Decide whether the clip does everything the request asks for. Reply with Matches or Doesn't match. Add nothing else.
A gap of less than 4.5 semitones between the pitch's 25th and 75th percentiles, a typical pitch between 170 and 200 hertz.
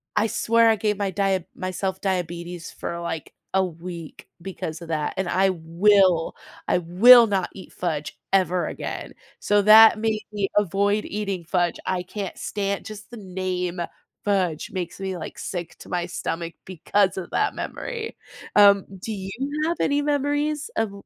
Matches